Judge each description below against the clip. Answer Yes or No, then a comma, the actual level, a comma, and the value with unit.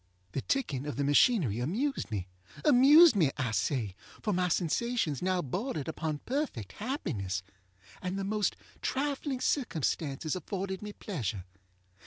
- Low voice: No, medium, 180 Hz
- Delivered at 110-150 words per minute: Yes, slow, 135 wpm